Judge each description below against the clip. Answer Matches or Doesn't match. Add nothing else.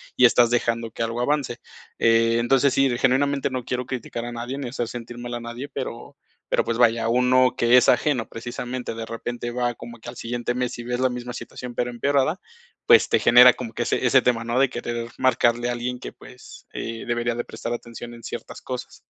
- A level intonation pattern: Matches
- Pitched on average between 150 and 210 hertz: Doesn't match